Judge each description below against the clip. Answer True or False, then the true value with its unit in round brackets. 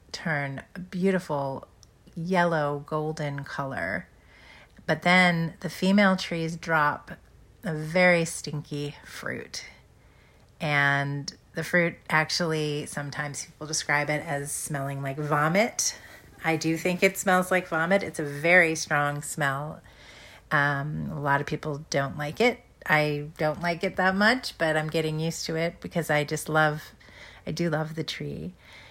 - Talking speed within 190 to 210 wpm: False (145 wpm)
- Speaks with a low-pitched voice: False (155 Hz)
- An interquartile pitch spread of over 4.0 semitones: False (2.8 semitones)